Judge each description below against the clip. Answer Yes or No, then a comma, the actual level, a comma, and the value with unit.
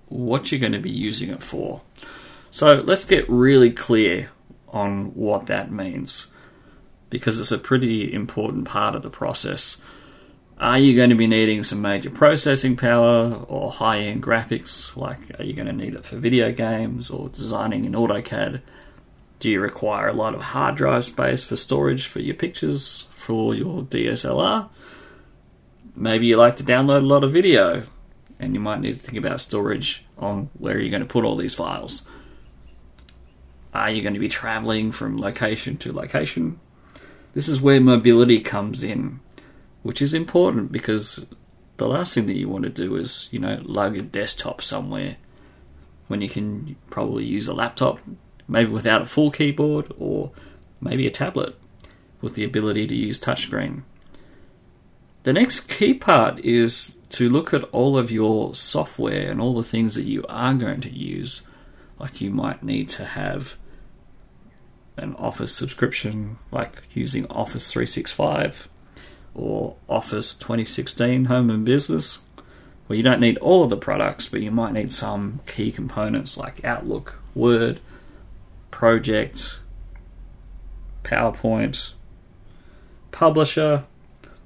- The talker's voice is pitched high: No, low, 115 Hz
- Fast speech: No, average, 155 wpm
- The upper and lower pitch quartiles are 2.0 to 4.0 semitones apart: Yes, average, 3.6 semitones